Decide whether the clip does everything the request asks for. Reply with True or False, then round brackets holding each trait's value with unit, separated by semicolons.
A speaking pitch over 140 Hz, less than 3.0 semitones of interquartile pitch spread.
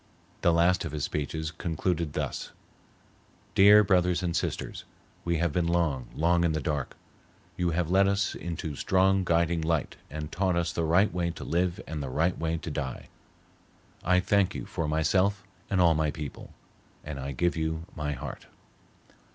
False (85 Hz; 2.6 semitones)